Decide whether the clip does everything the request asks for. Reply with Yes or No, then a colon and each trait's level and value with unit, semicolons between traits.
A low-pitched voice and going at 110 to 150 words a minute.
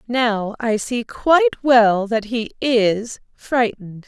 No: high, 235 Hz; slow, 135 wpm